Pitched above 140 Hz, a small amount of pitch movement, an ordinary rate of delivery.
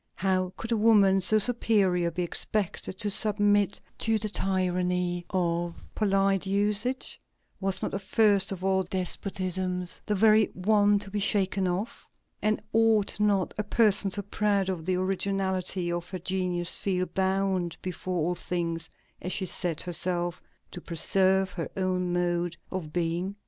Yes: high, 190 Hz; narrow, 2.2 semitones; average, 150 wpm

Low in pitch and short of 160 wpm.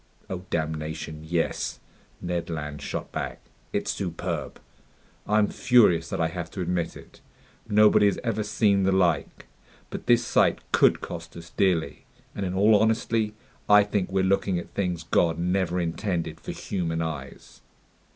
Yes: very low, 90 Hz; average, 150 wpm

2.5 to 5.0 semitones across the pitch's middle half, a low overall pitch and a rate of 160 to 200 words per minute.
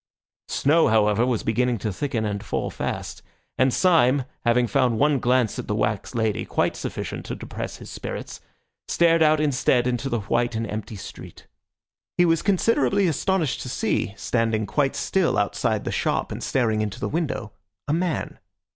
No: wide, 5.6 semitones; low, 125 Hz; average, 165 wpm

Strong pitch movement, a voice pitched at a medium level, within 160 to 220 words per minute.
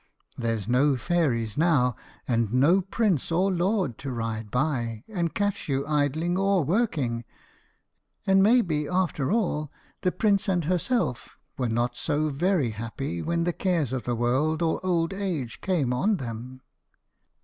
No: wide, 6.7 semitones; medium, 150 Hz; average, 150 wpm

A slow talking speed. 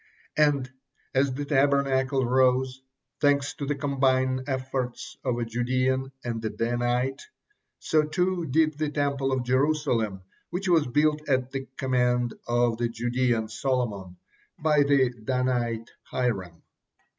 Yes: slow, 130 wpm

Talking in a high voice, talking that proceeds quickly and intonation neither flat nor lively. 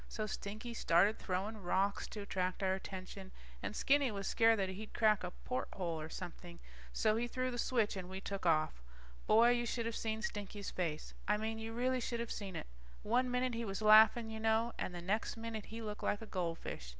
Yes: high, 215 Hz; fast, 210 wpm; average, 3.3 semitones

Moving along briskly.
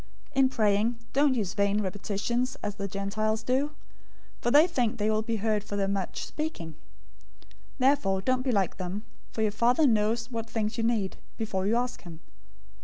No: average, 190 wpm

